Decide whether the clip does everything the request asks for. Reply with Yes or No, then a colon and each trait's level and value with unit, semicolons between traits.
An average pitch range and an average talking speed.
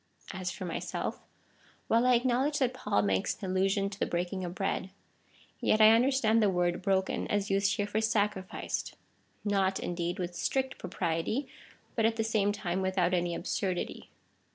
Yes: average, 3.5 semitones; average, 175 wpm